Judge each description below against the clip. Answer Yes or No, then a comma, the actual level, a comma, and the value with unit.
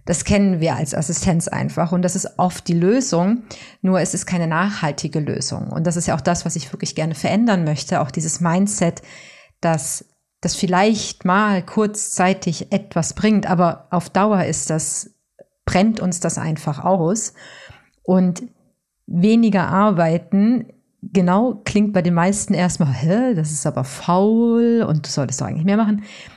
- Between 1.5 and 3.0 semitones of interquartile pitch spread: No, average, 3.6 semitones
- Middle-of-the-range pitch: Yes, medium, 180 Hz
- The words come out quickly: No, average, 160 wpm